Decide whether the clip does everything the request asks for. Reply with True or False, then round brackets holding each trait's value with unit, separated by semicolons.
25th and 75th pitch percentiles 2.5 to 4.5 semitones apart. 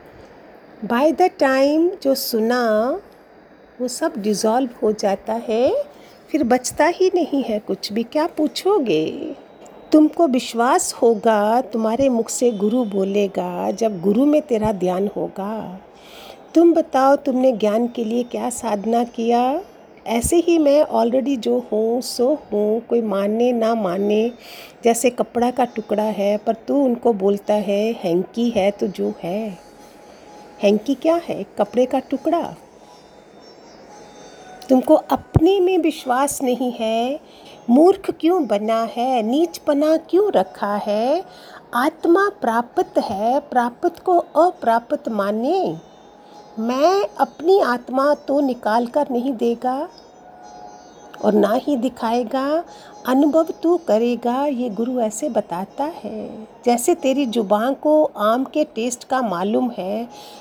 False (5.0 semitones)